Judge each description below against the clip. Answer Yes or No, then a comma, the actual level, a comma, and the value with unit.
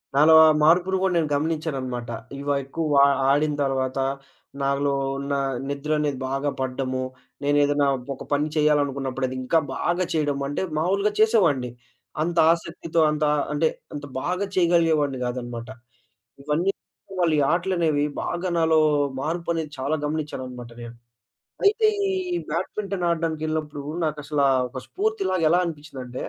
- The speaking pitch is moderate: Yes, medium, 150 Hz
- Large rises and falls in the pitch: No, average, 3.4 semitones